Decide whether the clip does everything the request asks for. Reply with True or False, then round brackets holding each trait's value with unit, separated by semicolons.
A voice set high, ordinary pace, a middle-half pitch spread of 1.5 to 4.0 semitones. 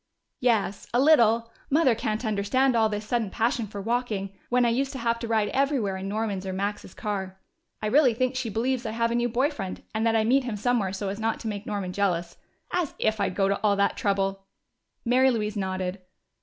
False (220 Hz; 220 wpm; 3.4 semitones)